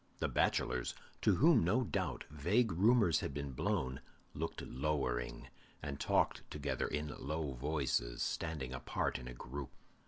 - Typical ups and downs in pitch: Yes, average, 4.2 semitones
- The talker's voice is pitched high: No, very low, 75 Hz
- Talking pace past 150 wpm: No, average, 145 wpm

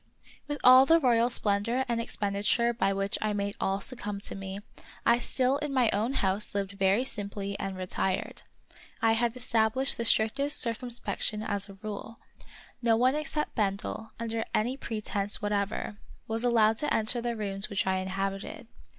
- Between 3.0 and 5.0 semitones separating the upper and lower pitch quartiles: Yes, average, 3.3 semitones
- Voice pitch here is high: Yes, high, 220 Hz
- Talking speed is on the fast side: No, average, 170 wpm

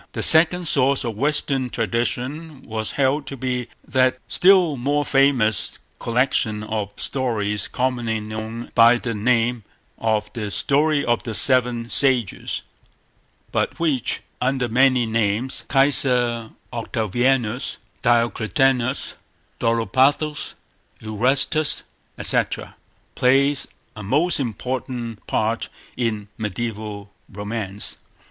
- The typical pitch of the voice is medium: No, low, 120 Hz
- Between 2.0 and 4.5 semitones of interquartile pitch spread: Yes, average, 3.4 semitones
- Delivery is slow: Yes, slow, 95 wpm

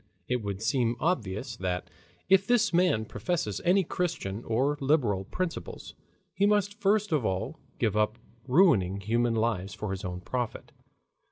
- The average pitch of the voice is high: No, low, 120 Hz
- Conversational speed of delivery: Yes, average, 150 wpm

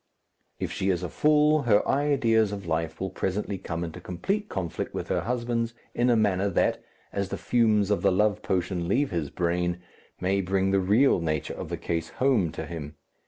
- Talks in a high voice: No, low, 100 Hz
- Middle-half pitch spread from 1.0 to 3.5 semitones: No, average, 4.8 semitones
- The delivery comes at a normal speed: Yes, average, 195 wpm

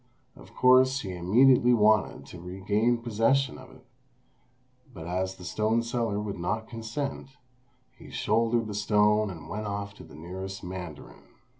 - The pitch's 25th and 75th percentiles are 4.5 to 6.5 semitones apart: No, average, 3.8 semitones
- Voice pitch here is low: Yes, low, 105 Hz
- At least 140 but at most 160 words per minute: Yes, average, 150 wpm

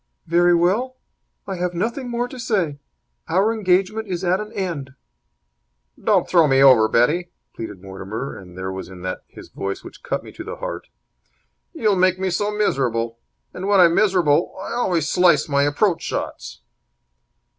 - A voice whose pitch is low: No, medium, 175 Hz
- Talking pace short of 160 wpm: No, average, 165 wpm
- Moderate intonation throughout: No, wide, 6.5 semitones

